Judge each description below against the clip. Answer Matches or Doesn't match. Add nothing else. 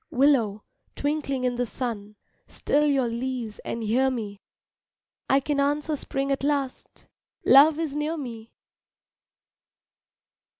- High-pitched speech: Matches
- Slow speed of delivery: Matches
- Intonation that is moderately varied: Matches